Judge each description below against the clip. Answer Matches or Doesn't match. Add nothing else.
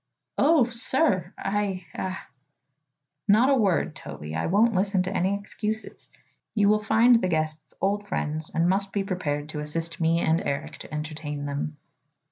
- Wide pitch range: Doesn't match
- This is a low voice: Doesn't match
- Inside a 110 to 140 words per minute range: Doesn't match